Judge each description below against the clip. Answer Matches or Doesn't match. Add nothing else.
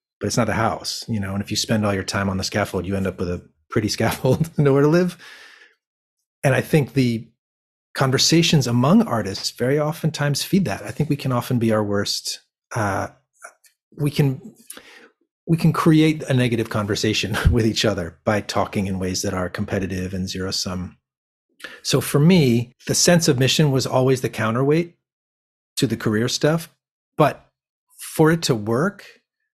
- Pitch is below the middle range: Matches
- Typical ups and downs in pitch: Doesn't match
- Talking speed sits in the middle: Matches